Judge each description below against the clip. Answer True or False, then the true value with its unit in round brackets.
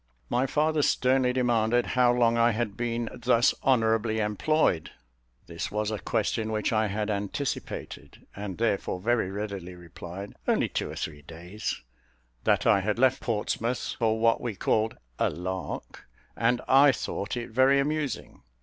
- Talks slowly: False (150 wpm)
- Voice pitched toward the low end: True (115 Hz)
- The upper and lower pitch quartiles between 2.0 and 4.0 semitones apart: True (3.3 semitones)